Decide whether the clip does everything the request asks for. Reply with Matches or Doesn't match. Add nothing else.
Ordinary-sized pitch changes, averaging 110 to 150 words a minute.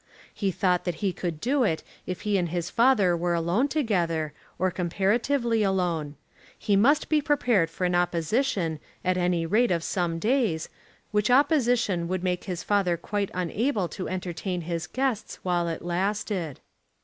Doesn't match